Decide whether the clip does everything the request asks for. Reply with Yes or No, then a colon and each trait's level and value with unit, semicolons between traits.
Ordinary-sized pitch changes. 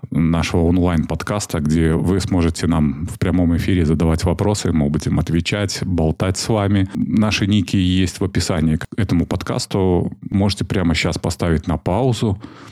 Yes: average, 3.4 semitones